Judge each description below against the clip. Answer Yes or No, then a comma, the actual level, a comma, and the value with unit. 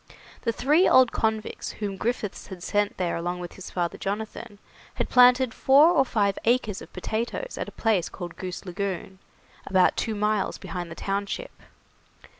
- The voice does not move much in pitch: No, average, 4.0 semitones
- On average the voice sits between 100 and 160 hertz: No, high, 205 Hz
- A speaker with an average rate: Yes, average, 165 wpm